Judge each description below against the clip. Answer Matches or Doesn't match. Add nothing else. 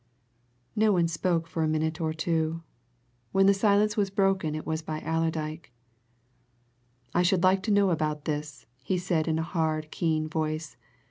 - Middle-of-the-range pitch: Matches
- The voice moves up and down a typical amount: Matches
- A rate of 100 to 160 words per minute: Doesn't match